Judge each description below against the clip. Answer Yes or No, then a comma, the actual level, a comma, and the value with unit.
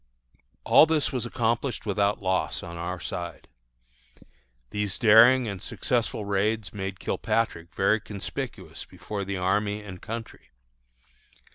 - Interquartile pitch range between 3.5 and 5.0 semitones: No, average, 2.8 semitones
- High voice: No, low, 105 Hz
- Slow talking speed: Yes, slow, 120 wpm